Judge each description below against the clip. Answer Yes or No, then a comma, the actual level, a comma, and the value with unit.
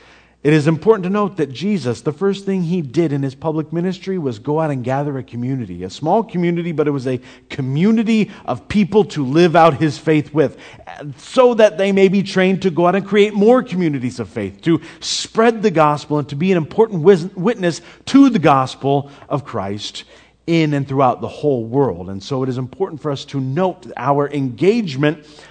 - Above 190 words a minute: Yes, average, 200 wpm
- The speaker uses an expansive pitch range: Yes, wide, 5.7 semitones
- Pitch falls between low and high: Yes, medium, 160 Hz